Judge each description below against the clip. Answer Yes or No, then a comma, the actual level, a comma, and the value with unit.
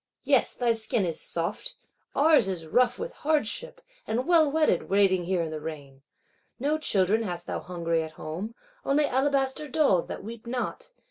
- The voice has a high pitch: Yes, high, 225 Hz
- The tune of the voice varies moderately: No, wide, 8.6 semitones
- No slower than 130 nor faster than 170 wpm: Yes, average, 165 wpm